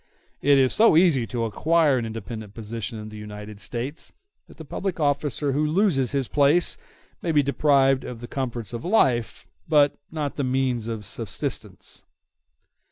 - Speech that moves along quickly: No, average, 165 wpm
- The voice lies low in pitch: Yes, low, 130 Hz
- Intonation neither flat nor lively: Yes, average, 4.5 semitones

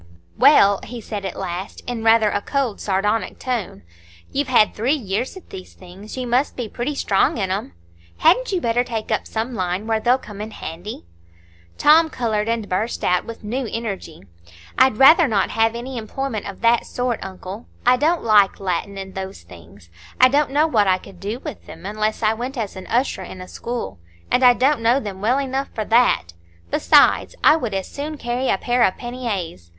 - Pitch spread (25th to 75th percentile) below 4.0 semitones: No, average, 4.4 semitones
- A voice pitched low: No, high, 225 Hz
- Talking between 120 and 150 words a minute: No, average, 195 wpm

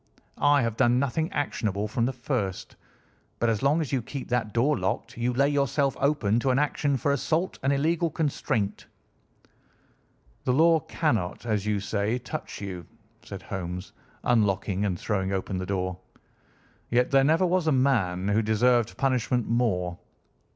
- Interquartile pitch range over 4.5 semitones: Yes, wide, 5.6 semitones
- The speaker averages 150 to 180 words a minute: Yes, average, 160 wpm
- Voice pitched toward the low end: Yes, low, 120 Hz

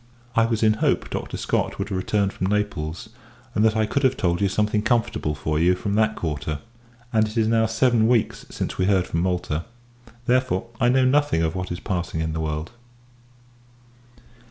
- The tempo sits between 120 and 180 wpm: No, average, 195 wpm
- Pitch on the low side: Yes, low, 105 Hz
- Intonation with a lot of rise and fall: No, average, 4.6 semitones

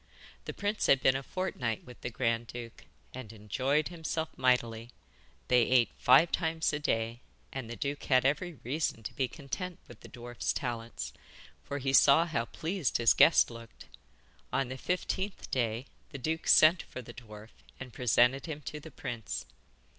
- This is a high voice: No, low, 130 Hz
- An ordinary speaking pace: Yes, average, 170 wpm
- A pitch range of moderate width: Yes, average, 4.5 semitones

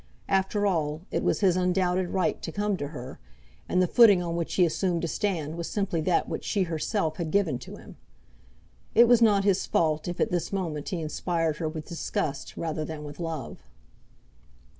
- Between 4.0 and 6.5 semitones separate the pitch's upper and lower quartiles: No, average, 3.5 semitones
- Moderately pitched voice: Yes, medium, 170 Hz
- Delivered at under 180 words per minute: No, average, 195 wpm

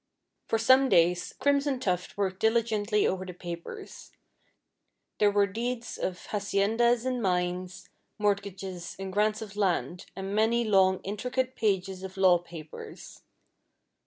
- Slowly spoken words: Yes, slow, 130 wpm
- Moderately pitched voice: No, high, 200 Hz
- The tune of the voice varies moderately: Yes, average, 3.3 semitones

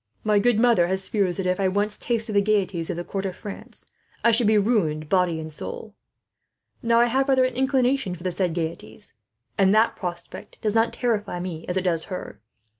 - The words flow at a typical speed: No, fast, 210 wpm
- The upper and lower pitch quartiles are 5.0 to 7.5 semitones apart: No, average, 4.3 semitones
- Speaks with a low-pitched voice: No, high, 200 Hz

